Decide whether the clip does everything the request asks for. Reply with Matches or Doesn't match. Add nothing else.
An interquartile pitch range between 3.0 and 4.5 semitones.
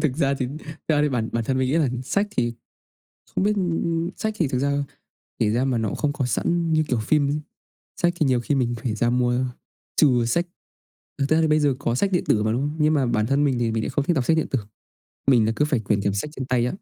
Matches